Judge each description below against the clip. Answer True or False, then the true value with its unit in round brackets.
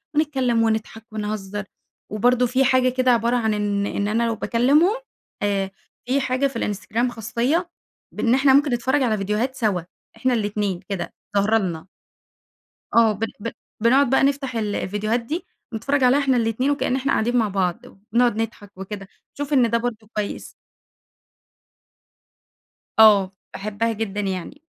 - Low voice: False (230 Hz)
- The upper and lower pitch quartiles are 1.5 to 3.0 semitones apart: False (3.7 semitones)